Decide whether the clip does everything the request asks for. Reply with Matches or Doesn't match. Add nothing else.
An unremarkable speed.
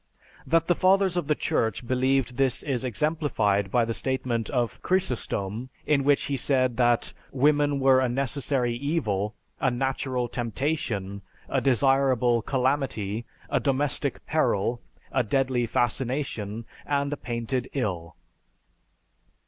Doesn't match